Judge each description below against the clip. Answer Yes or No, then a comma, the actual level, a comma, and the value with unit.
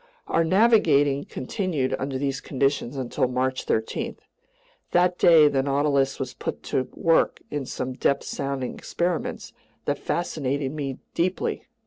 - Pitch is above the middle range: No, medium, 140 Hz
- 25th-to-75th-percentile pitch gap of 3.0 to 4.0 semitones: Yes, average, 3.6 semitones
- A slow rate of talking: Yes, slow, 130 wpm